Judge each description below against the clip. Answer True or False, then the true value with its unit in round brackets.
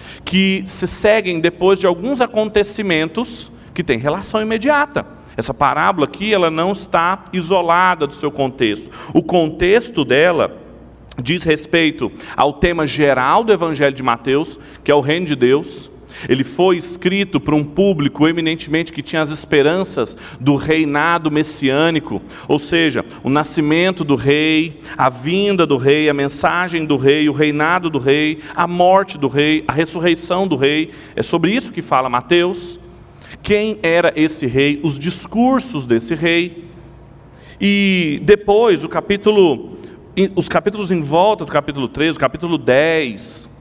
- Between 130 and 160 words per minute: True (145 wpm)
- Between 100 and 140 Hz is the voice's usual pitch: False (165 Hz)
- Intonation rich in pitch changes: False (3.8 semitones)